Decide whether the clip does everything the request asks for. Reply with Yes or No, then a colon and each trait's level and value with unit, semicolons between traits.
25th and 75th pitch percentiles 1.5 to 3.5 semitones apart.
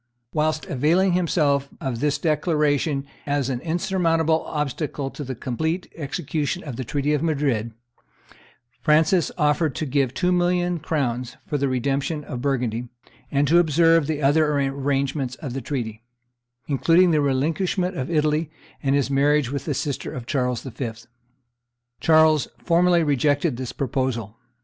Yes: average, 3.0 semitones